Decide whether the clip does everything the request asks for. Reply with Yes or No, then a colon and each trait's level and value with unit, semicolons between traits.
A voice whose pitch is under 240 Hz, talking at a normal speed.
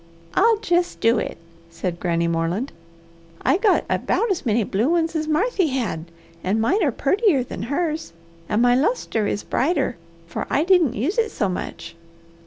No: very high, 270 Hz; average, 170 wpm